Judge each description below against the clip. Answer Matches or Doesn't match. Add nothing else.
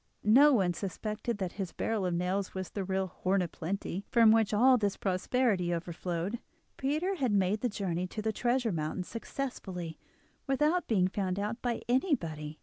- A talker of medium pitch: Doesn't match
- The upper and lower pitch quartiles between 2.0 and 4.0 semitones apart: Doesn't match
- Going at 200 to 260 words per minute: Doesn't match